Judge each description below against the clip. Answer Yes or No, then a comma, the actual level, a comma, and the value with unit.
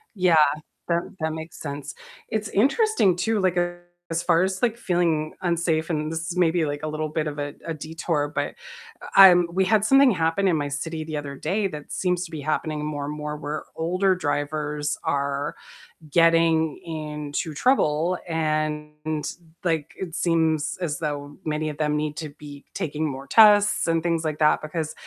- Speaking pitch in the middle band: Yes, medium, 160 Hz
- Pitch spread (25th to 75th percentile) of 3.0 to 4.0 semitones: No, narrow, 2.6 semitones